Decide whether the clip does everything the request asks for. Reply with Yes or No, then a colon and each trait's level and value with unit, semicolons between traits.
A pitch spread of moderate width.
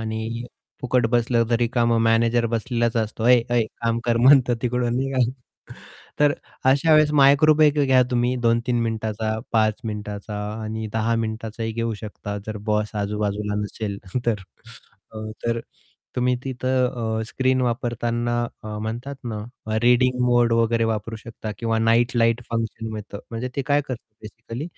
No: narrow, 1.9 semitones